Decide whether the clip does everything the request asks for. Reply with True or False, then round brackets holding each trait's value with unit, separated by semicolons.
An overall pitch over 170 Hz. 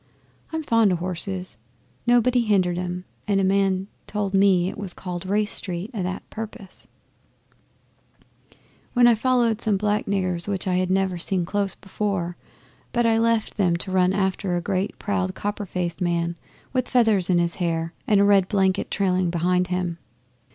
True (190 Hz)